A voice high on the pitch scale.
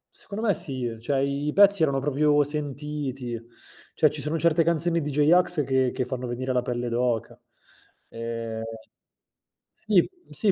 No: medium, 140 Hz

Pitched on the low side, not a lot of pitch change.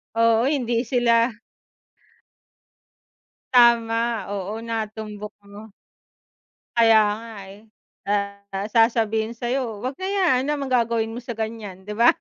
No: high, 225 Hz; narrow, 2.2 semitones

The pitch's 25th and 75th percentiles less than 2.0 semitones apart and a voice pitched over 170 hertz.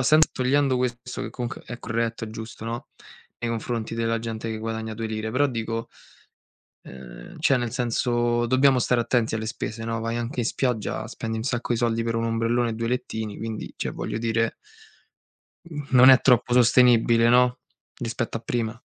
No: narrow, 1.5 semitones; low, 115 Hz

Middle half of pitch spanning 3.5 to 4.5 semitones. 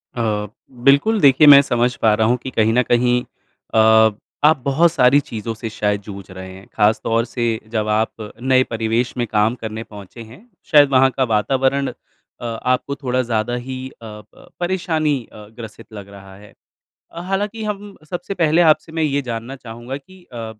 Yes: average, 4.2 semitones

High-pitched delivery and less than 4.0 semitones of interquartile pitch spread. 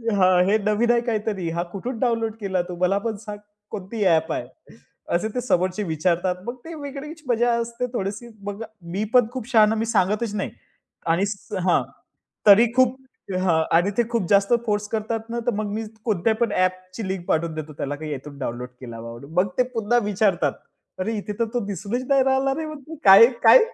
No: high, 210 Hz; average, 4.3 semitones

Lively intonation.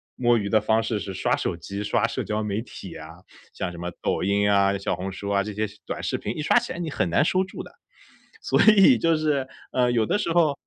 Yes: wide, 6.4 semitones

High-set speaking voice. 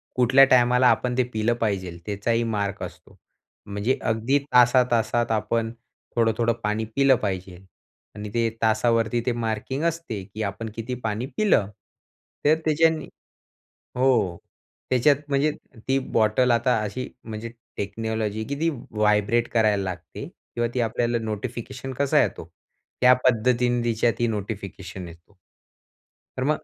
No: low, 115 Hz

